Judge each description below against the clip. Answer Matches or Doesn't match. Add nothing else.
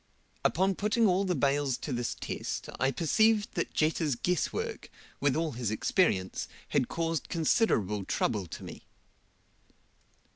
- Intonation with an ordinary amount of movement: Doesn't match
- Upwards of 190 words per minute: Doesn't match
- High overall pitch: Doesn't match